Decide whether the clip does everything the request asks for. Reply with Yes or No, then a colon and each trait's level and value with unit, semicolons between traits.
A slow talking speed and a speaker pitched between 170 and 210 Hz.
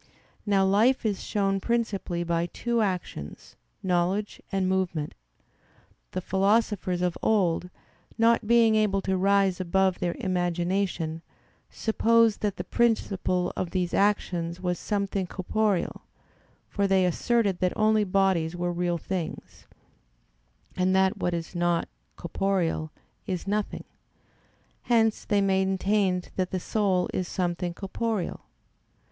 Yes: slow, 120 wpm; high, 190 Hz